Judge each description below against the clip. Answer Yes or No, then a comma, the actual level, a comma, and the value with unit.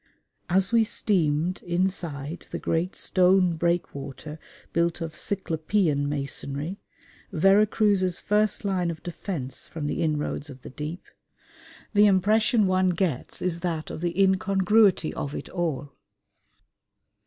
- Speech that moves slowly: Yes, slow, 125 wpm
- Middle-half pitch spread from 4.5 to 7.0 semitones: No, average, 3.9 semitones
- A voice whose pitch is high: No, medium, 175 Hz